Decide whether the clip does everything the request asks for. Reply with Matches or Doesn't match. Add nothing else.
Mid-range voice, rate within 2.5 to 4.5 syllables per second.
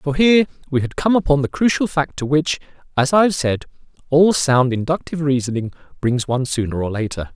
Doesn't match